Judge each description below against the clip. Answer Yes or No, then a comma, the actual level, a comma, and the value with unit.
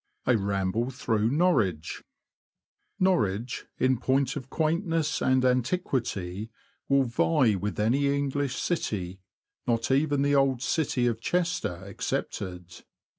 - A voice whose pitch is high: No, low, 125 Hz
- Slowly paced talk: Yes, slow, 125 wpm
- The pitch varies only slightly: No, wide, 5.4 semitones